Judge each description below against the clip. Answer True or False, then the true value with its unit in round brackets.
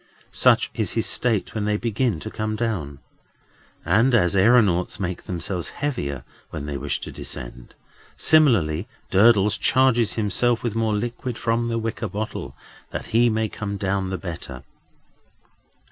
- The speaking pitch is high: False (105 Hz)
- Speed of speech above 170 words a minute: False (145 wpm)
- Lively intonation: False (4.3 semitones)